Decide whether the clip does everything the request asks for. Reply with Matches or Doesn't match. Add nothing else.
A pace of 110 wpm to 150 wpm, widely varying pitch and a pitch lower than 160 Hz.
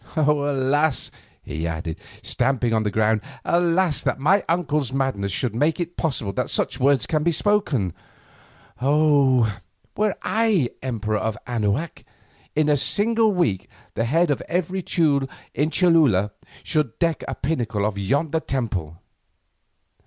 Matches